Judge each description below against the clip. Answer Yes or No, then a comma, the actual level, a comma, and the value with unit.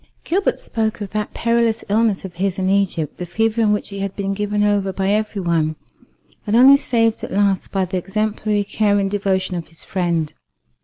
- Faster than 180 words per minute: Yes, average, 200 wpm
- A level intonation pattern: Yes, narrow, 2.3 semitones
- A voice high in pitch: Yes, high, 200 Hz